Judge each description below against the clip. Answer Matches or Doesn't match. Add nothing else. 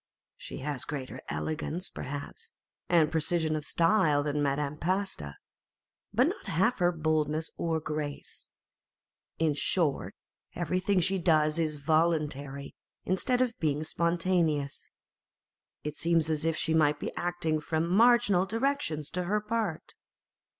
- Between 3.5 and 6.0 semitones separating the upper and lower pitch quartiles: Doesn't match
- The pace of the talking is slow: Matches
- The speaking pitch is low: Doesn't match